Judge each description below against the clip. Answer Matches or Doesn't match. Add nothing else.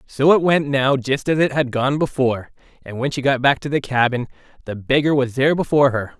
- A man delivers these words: Matches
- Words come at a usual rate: Doesn't match